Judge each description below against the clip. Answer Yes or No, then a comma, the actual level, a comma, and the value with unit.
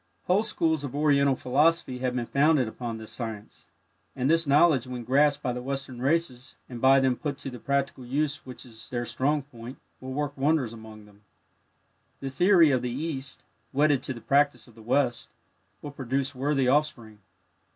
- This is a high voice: No, low, 135 Hz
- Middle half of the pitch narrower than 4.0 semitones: Yes, average, 2.9 semitones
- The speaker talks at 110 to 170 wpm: No, average, 185 wpm